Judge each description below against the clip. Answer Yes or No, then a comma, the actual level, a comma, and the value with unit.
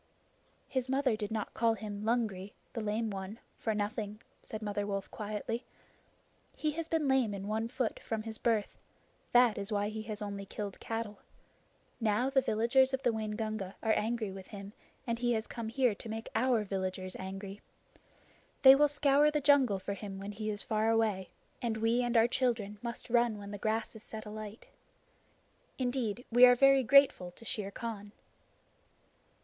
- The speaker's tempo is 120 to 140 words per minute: No, average, 175 wpm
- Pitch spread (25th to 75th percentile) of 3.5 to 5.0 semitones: No, average, 2.8 semitones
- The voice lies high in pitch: Yes, high, 220 Hz